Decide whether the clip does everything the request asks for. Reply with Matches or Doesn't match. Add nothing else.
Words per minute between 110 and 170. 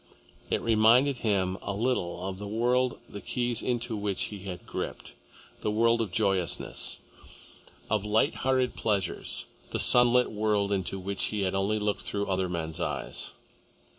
Matches